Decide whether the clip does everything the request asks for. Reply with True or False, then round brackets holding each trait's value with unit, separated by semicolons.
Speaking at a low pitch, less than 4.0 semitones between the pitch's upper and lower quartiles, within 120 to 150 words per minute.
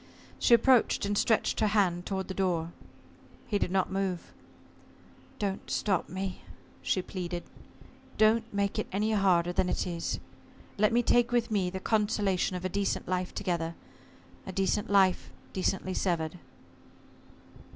False (190 Hz; 2.5 semitones; 145 wpm)